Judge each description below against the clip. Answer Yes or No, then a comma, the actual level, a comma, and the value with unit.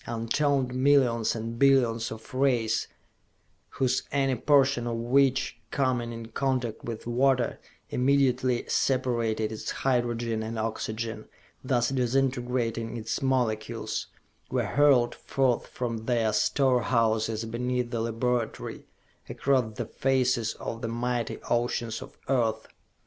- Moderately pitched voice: No, low, 120 Hz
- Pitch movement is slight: Yes, narrow, 2.3 semitones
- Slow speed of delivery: Yes, slow, 115 wpm